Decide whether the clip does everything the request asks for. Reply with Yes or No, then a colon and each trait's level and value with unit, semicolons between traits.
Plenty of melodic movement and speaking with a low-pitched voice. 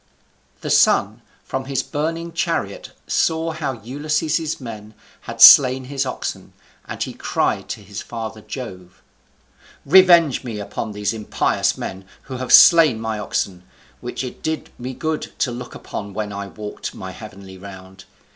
Yes: wide, 6.3 semitones; low, 125 Hz